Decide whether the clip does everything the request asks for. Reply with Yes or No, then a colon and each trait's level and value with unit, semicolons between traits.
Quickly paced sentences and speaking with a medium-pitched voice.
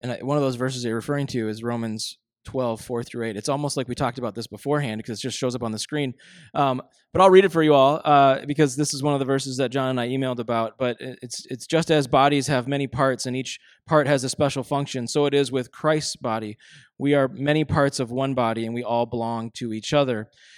No: fast, 260 wpm; low, 130 Hz